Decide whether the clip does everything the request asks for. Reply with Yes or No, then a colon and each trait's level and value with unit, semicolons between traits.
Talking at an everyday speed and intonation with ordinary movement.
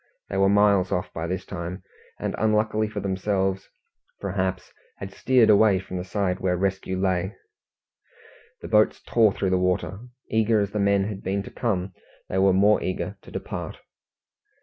No: average, 170 wpm; narrow, 2.0 semitones